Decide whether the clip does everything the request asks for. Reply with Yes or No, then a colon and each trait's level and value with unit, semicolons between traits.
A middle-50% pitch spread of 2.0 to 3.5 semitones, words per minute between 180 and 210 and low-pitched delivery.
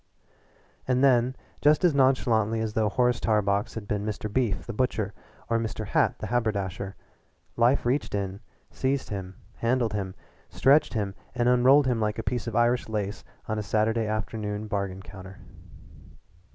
No: average, 3.0 semitones; average, 165 wpm; low, 110 Hz